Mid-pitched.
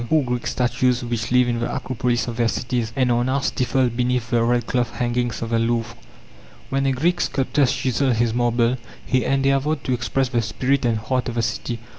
No: low, 125 Hz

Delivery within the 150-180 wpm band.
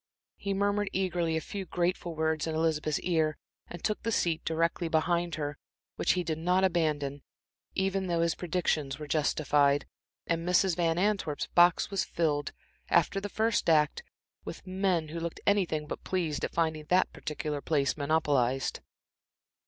Yes: average, 160 wpm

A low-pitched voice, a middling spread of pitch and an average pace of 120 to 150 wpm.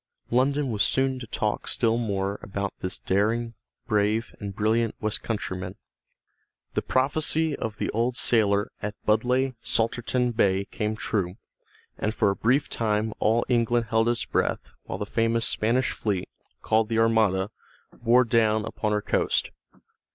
No: low, 110 Hz; narrow, 2.3 semitones; average, 145 wpm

